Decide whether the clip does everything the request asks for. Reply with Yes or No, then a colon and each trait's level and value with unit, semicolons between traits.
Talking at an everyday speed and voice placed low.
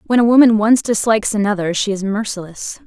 No: average, 190 wpm; high, 215 Hz